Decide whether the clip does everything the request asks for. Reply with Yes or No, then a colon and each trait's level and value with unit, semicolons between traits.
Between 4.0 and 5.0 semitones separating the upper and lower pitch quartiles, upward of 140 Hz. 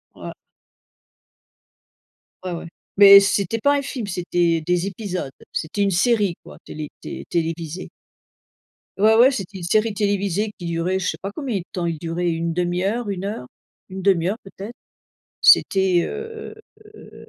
No: average, 3.3 semitones; high, 190 Hz